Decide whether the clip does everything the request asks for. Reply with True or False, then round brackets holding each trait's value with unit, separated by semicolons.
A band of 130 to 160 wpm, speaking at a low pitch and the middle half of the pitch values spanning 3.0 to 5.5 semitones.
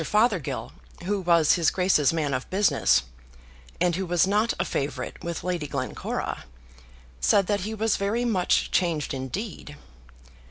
False (145 wpm; 180 Hz; 5.1 semitones)